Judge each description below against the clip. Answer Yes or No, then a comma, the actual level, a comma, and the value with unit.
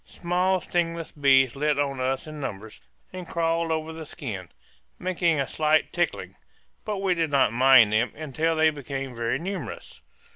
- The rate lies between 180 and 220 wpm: No, average, 160 wpm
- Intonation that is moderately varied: Yes, average, 4.0 semitones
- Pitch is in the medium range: Yes, medium, 155 Hz